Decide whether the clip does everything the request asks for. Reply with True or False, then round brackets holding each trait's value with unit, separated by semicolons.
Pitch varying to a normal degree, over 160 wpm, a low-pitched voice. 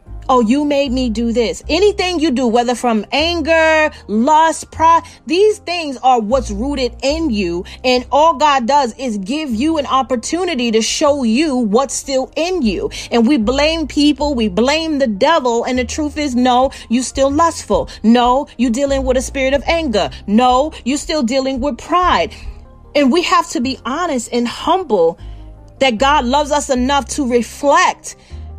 False (3.9 semitones; 170 wpm; 270 Hz)